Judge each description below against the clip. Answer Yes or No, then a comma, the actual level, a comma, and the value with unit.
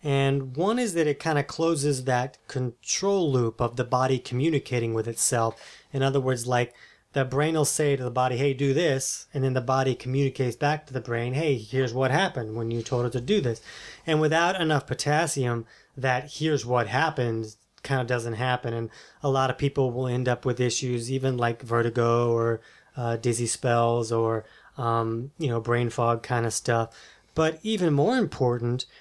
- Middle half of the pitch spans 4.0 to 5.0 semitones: No, average, 3.3 semitones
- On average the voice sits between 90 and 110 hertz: No, low, 130 Hz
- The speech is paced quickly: No, average, 190 wpm